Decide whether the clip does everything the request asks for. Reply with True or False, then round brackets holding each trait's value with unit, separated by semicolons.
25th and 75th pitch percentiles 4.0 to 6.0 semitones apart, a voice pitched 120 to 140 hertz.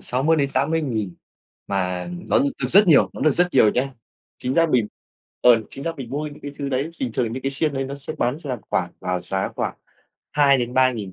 False (3.5 semitones; 135 Hz)